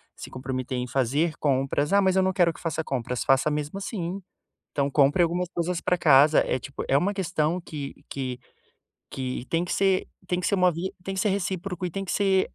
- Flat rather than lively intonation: No, average, 5.1 semitones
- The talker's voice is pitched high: No, medium, 165 Hz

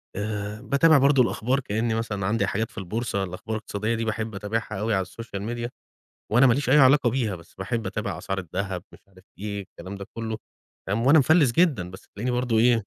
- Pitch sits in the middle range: No, low, 110 Hz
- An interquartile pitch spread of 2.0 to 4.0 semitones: Yes, average, 3.7 semitones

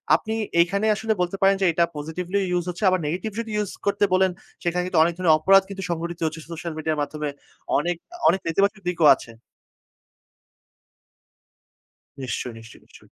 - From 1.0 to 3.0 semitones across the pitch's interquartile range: No, average, 3.4 semitones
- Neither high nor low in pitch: Yes, medium, 175 Hz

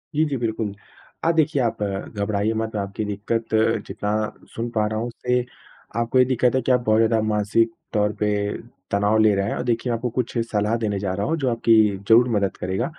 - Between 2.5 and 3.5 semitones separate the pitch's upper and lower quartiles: Yes, average, 2.8 semitones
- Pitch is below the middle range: Yes, low, 110 Hz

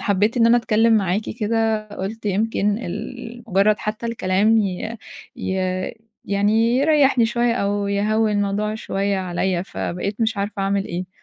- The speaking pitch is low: No, high, 210 Hz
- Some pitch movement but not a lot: No, narrow, 2.3 semitones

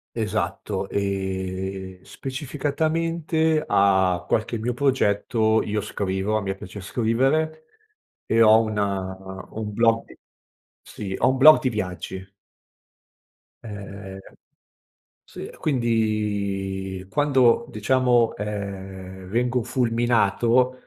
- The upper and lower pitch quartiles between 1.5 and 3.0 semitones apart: No, average, 4.3 semitones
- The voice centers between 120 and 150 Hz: No, low, 110 Hz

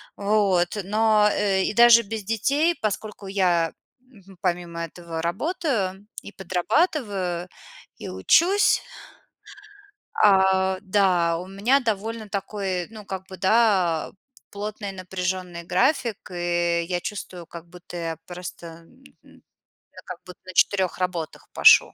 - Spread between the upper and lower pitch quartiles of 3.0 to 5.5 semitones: Yes, average, 3.3 semitones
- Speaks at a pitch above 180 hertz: Yes, high, 190 Hz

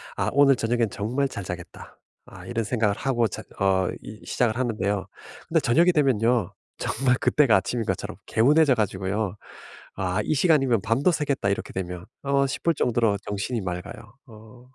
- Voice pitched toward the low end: Yes, low, 115 Hz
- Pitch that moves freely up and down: No, average, 5.0 semitones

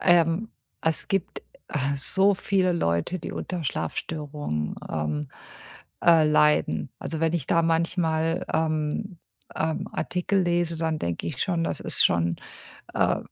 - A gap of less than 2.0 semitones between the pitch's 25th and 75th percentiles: No, average, 2.7 semitones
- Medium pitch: Yes, medium, 160 Hz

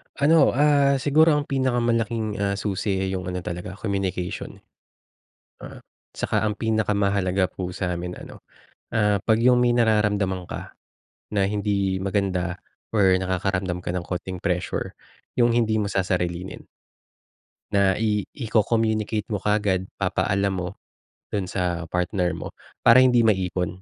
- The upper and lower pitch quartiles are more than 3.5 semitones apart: No, average, 3.1 semitones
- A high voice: No, low, 100 Hz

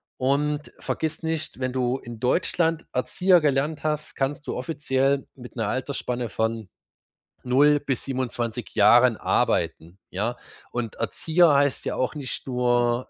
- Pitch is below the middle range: Yes, low, 130 Hz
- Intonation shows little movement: No, average, 3.4 semitones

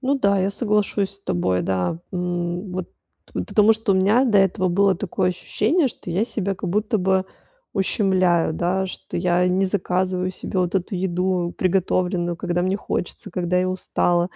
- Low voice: No, medium, 185 Hz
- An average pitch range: No, narrow, 2.0 semitones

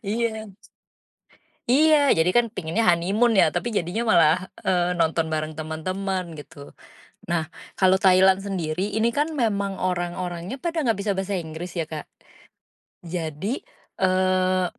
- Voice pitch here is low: No, medium, 185 Hz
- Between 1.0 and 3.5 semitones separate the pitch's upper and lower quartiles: No, average, 4.0 semitones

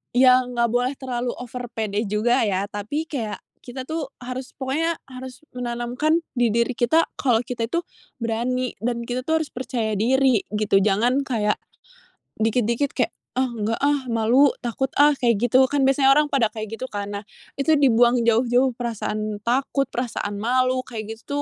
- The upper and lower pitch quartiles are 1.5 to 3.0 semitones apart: Yes, average, 2.7 semitones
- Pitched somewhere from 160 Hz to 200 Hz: No, high, 245 Hz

